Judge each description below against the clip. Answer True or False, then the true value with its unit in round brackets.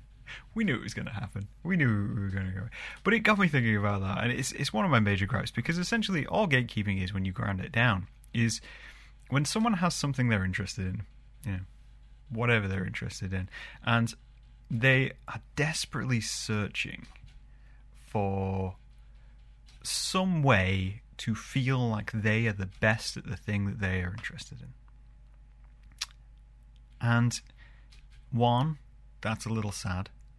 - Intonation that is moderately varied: True (4.0 semitones)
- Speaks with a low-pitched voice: True (115 Hz)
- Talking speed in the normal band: True (160 wpm)